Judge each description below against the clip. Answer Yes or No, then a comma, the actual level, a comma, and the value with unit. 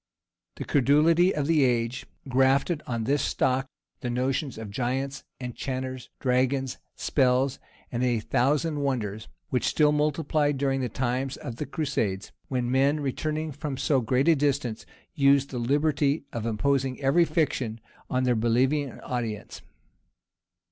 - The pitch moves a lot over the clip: No, narrow, 2.6 semitones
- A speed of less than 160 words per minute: Yes, average, 140 wpm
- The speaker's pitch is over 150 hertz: No, low, 135 Hz